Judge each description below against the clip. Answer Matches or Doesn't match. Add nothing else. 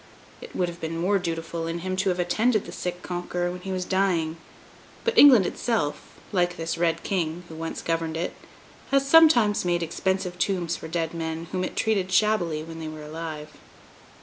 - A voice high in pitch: Doesn't match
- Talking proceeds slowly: Doesn't match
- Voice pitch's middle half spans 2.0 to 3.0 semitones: Matches